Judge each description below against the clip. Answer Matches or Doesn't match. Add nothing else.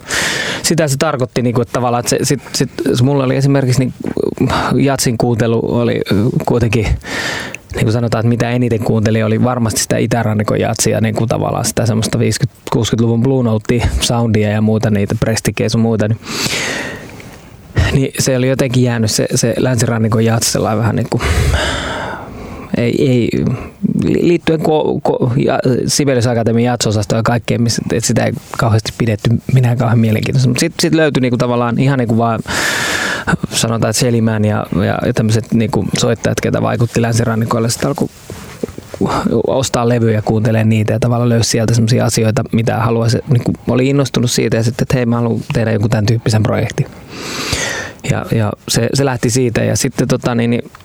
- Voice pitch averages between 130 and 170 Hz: Doesn't match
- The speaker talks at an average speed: Doesn't match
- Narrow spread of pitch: Matches